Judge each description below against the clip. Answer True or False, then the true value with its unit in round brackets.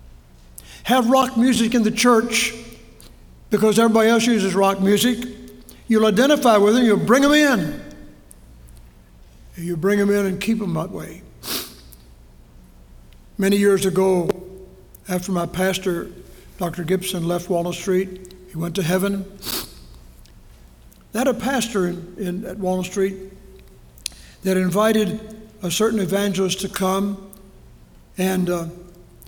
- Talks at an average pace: False (125 wpm)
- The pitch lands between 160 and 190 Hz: True (185 Hz)